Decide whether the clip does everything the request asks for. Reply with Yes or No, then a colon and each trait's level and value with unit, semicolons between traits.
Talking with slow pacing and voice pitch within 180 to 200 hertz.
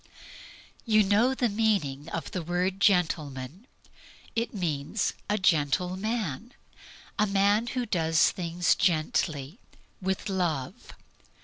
Yes: slow, 110 wpm; medium, 185 Hz